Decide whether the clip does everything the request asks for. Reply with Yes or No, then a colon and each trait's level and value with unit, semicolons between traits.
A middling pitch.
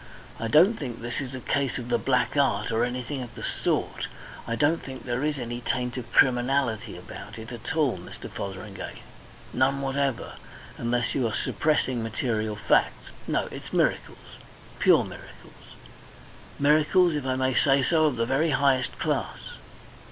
No: low, 130 Hz